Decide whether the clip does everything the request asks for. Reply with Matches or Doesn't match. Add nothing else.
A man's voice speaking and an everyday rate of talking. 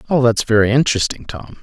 Matches